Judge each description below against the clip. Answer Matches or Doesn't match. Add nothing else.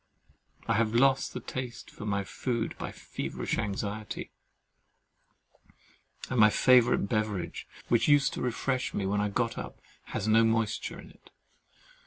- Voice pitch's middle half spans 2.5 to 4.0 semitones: Matches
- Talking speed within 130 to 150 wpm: Matches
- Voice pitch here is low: Matches